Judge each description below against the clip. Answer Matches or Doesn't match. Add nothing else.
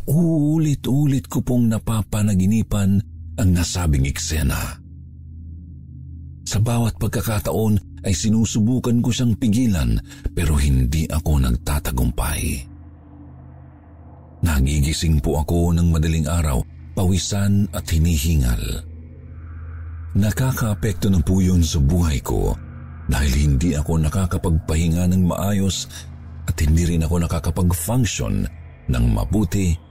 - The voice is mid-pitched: Doesn't match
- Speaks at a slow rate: Matches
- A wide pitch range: Doesn't match